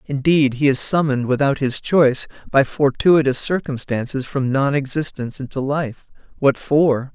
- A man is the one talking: Yes, male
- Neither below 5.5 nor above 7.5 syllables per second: No, 4.8 syllables/s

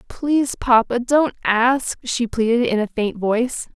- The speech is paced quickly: No, average, 160 wpm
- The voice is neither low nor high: No, high, 240 Hz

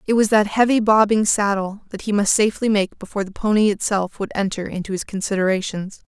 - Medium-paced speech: Yes, average, 195 wpm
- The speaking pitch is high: Yes, high, 205 Hz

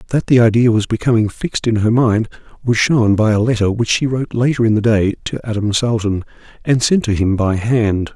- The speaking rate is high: Yes, fast, 220 wpm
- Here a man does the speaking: Yes, male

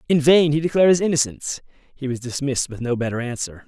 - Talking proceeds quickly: Yes, fast, 210 wpm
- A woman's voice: No, male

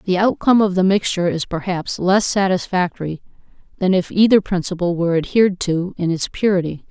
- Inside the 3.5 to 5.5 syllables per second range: No, 5.8 syllables/s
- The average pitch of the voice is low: No, medium, 185 Hz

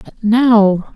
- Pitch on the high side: Yes, high, 220 Hz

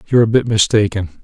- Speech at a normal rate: Yes, average, 195 wpm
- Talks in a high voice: No, low, 110 Hz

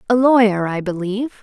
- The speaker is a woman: Yes, female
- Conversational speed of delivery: Yes, average, 170 wpm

